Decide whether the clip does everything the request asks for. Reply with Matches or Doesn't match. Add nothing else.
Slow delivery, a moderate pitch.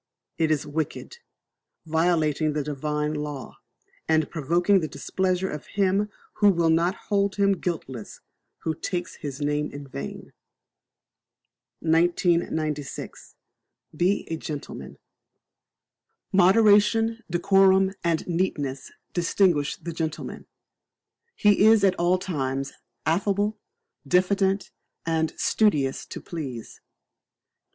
Matches